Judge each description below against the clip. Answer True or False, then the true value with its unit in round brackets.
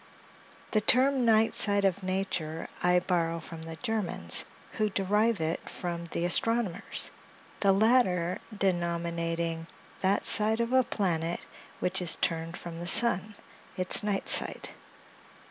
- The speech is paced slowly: True (130 wpm)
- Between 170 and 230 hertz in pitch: True (185 Hz)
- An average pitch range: True (4.0 semitones)